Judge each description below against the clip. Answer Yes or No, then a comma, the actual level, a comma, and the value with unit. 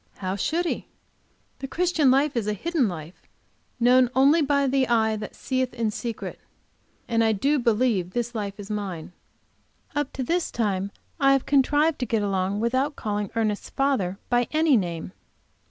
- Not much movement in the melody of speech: No, average, 4.9 semitones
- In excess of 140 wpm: Yes, average, 165 wpm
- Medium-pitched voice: No, high, 240 Hz